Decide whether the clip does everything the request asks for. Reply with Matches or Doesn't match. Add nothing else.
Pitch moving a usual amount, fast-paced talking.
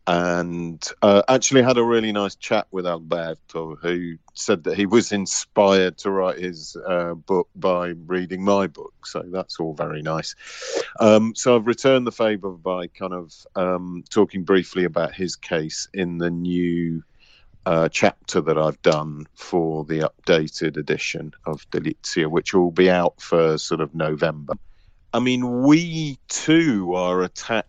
Doesn't match